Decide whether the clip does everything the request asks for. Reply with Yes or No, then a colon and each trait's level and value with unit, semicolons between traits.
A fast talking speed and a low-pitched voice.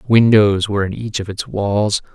No: average, 195 wpm; low, 105 Hz